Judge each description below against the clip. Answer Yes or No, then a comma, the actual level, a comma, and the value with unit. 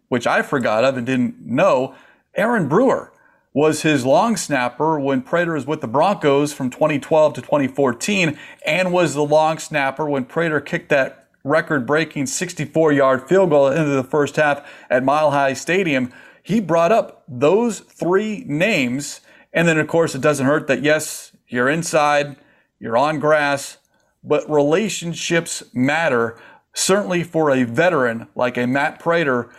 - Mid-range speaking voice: Yes, medium, 150 Hz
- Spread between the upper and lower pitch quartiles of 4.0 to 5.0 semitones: No, average, 3.6 semitones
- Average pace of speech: Yes, average, 155 wpm